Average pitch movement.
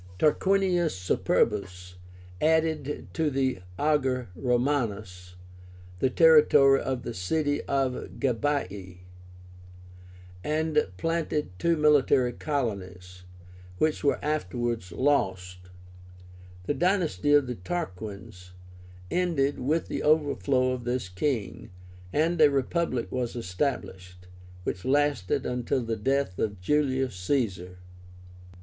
No: wide, 7.2 semitones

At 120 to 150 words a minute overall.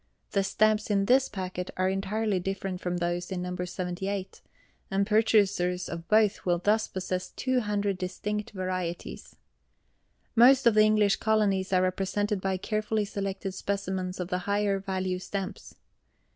Yes: average, 145 wpm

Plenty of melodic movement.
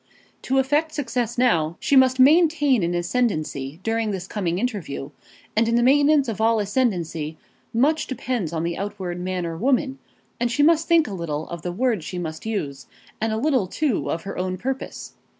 Yes: wide, 7.1 semitones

